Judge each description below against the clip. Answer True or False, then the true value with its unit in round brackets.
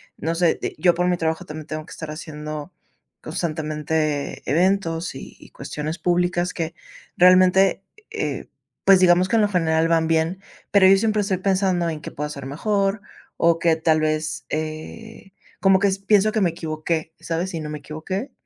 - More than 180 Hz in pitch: False (165 Hz)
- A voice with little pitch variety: False (3.2 semitones)